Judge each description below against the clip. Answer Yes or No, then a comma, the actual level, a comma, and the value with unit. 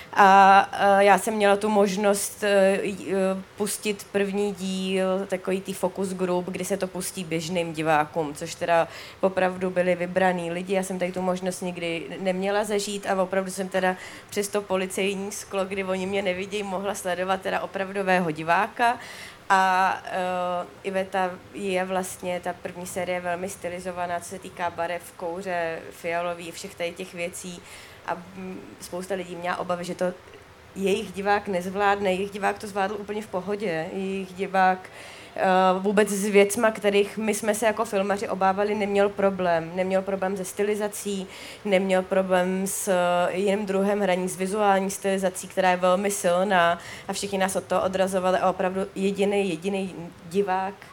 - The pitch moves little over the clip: Yes, narrow, 1.5 semitones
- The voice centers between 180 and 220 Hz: Yes, high, 190 Hz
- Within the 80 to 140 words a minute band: No, average, 150 wpm